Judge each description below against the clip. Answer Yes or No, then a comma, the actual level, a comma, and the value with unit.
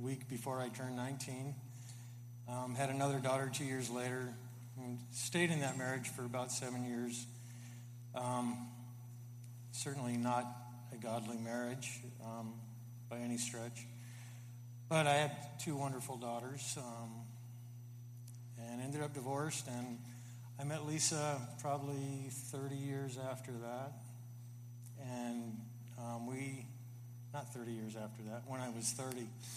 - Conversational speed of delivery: No, slow, 130 wpm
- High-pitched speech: No, low, 120 Hz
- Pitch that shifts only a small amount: Yes, narrow, 1.5 semitones